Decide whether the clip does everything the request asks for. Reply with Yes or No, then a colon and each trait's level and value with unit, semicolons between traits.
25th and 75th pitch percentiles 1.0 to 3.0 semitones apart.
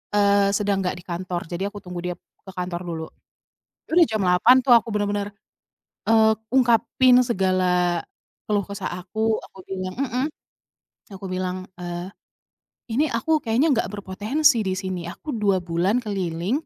No: average, 3.7 semitones